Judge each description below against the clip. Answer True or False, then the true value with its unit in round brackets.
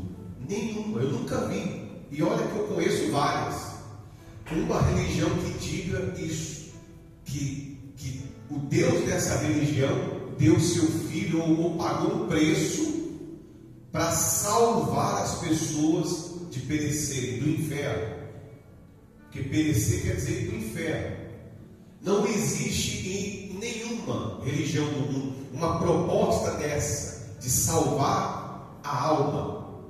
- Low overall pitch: False (150 Hz)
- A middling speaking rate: False (110 wpm)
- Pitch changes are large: False (4.8 semitones)